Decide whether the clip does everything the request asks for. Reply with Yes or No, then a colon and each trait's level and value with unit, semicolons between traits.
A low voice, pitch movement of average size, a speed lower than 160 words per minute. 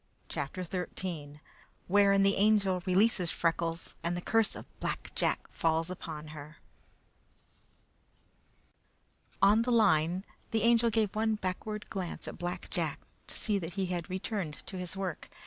No: medium, 185 Hz; average, 3.7 semitones; average, 145 wpm